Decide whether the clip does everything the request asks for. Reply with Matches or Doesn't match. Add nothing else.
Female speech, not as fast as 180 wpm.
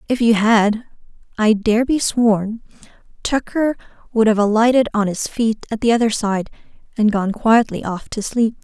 Matches